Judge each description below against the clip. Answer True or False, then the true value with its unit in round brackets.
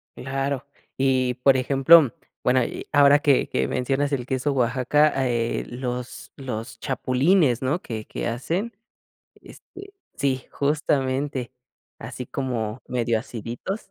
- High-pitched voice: False (130 Hz)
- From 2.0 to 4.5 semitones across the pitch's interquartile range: True (2.5 semitones)